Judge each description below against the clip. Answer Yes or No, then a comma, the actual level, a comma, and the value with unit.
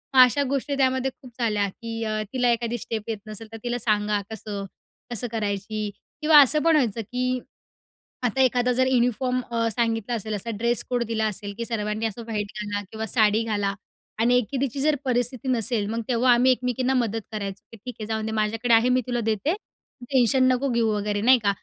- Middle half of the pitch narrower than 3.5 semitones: Yes, average, 2.8 semitones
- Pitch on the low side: No, high, 230 Hz